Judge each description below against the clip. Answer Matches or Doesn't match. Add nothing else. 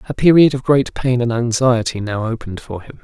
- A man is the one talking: Matches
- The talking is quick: Matches